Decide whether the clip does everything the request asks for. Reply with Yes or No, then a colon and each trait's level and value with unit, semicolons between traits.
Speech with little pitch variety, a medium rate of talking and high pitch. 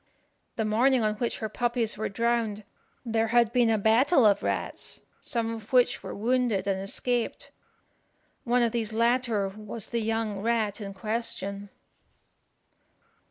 Yes: narrow, 2.0 semitones; average, 145 wpm; high, 225 Hz